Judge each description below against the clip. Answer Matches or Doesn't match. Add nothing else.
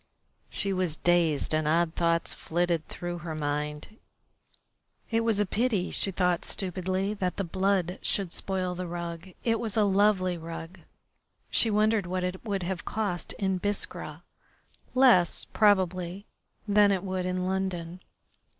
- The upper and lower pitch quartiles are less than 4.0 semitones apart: Matches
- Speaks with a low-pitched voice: Doesn't match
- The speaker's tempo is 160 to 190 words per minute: Doesn't match